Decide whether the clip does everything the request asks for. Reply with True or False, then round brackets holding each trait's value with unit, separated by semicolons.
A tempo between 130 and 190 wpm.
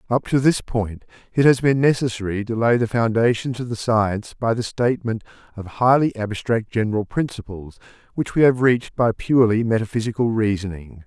True (170 wpm)